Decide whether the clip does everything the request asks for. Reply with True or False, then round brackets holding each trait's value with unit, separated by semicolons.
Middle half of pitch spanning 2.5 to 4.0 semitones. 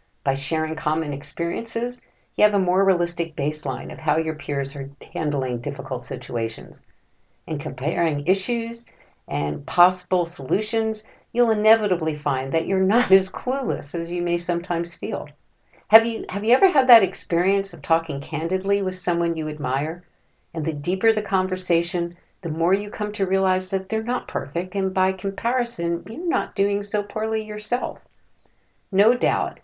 False (4.8 semitones)